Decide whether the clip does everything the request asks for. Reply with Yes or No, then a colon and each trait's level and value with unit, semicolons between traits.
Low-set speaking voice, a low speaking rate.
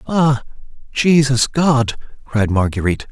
Yes: low, 130 Hz; slow, 95 wpm